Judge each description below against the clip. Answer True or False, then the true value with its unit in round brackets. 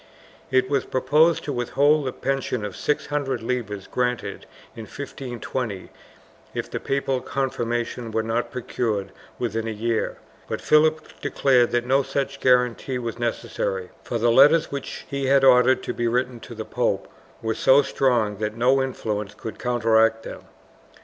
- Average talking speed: True (155 wpm)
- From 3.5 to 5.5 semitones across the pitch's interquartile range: False (3.1 semitones)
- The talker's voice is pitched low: True (125 Hz)